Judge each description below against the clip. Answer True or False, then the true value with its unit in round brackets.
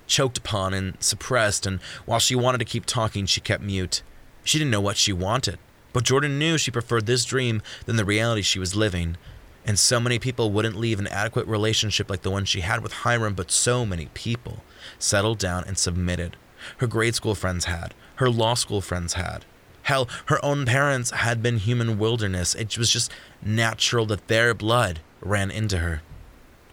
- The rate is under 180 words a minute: False (190 wpm)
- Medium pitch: False (110 Hz)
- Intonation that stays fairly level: False (3.7 semitones)